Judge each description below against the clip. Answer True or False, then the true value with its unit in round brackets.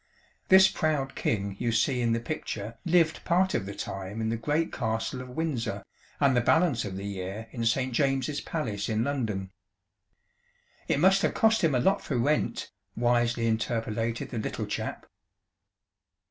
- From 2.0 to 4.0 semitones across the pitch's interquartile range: False (5.1 semitones)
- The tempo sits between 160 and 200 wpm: True (165 wpm)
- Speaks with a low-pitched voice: True (120 Hz)